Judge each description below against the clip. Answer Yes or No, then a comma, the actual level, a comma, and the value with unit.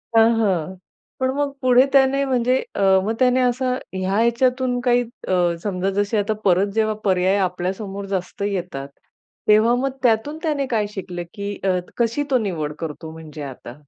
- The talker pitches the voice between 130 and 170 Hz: No, high, 215 Hz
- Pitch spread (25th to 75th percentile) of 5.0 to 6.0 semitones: Yes, average, 5.3 semitones